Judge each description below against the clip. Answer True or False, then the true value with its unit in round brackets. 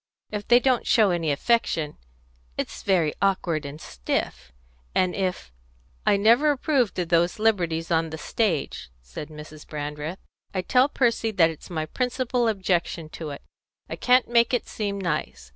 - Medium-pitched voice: True (180 Hz)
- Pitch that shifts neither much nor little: False (6.6 semitones)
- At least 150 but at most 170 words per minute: True (160 wpm)